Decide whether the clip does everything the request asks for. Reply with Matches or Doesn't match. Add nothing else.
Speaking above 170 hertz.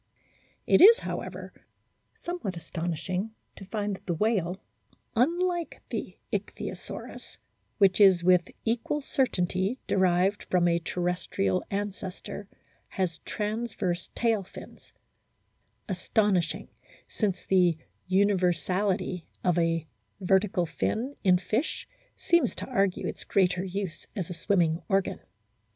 Matches